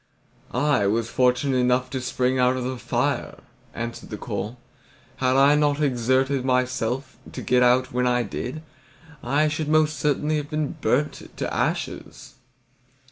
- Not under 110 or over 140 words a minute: No, average, 150 wpm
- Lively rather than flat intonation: No, narrow, 2.5 semitones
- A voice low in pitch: Yes, low, 130 Hz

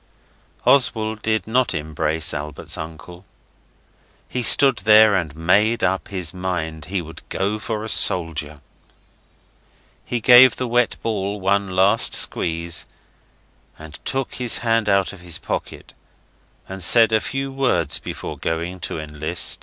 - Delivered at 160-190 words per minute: No, average, 140 wpm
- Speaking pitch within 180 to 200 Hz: No, very low, 95 Hz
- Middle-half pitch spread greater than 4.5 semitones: Yes, wide, 5.4 semitones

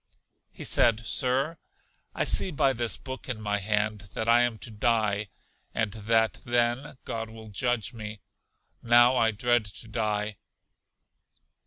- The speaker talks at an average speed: Yes, average, 145 wpm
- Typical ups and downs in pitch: No, narrow, 2.3 semitones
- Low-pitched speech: Yes, low, 115 Hz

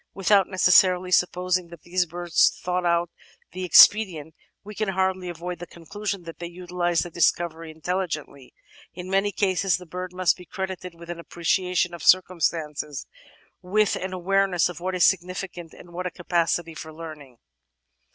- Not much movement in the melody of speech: Yes, narrow, 1.5 semitones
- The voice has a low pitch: No, medium, 180 Hz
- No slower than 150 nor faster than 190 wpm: Yes, average, 160 wpm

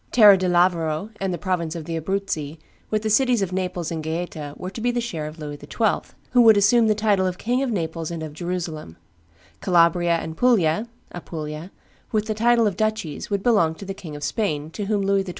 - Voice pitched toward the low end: No, medium, 185 Hz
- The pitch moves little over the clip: No, average, 4.8 semitones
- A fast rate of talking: Yes, fast, 220 wpm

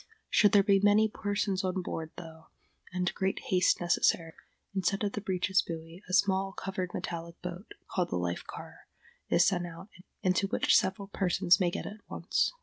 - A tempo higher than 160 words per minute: Yes, average, 175 wpm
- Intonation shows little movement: Yes, narrow, 2.2 semitones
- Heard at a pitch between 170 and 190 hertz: Yes, medium, 185 Hz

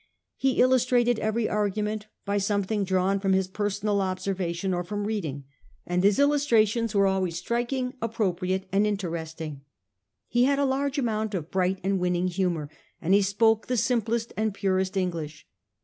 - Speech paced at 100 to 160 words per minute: Yes, average, 155 wpm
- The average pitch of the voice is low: No, high, 200 Hz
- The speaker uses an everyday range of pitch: Yes, average, 3.3 semitones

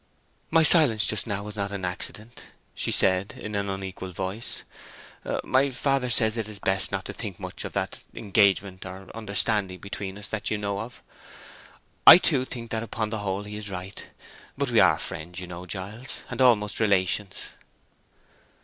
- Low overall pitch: Yes, low, 105 Hz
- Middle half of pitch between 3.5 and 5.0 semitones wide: No, average, 2.7 semitones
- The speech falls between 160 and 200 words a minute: Yes, average, 175 wpm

